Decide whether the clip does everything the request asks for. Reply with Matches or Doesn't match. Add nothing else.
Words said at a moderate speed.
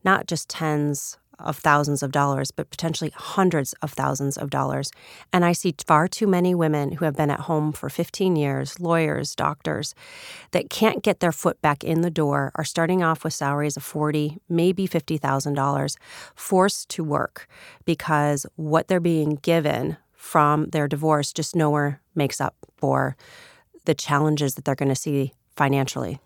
Matches